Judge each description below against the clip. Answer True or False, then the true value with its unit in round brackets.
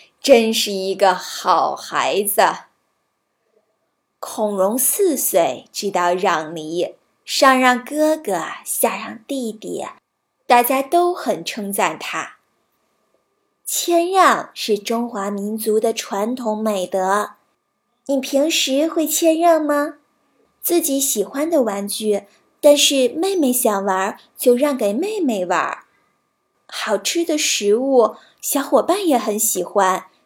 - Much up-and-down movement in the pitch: True (6.5 semitones)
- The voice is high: True (245 Hz)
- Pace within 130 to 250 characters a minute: True (160 characters per minute)